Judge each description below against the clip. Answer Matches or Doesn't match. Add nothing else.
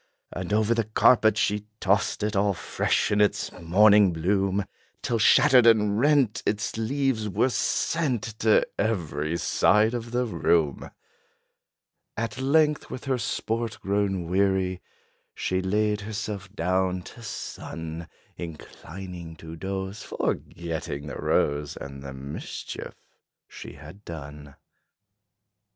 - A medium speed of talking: Doesn't match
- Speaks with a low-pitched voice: Matches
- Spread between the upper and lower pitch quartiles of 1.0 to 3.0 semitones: Doesn't match